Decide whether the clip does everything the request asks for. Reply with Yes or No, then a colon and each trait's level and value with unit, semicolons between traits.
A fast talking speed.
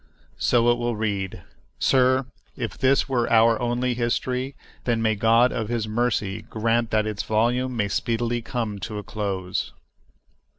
No: average, 155 wpm